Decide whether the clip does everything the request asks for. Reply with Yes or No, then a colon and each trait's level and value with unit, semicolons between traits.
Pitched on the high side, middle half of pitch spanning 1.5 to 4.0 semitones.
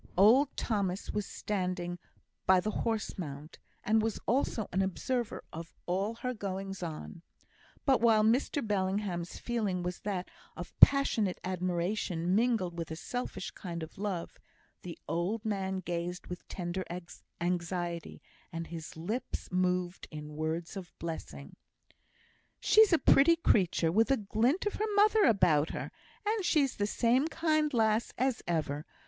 No: high, 195 Hz; average, 4.9 semitones